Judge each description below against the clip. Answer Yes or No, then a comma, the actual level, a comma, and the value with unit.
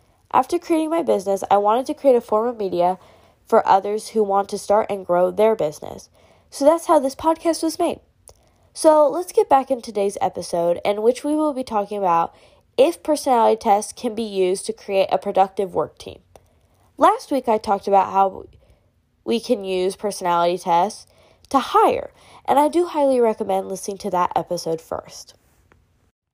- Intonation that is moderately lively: No, wide, 6.5 semitones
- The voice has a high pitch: Yes, high, 210 Hz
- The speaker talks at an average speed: No, fast, 180 wpm